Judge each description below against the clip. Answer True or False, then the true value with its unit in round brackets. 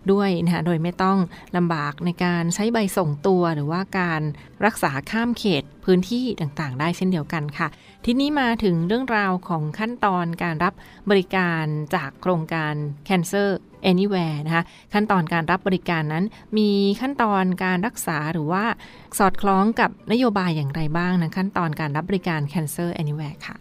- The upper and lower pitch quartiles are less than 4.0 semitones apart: True (3.3 semitones)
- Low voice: False (180 Hz)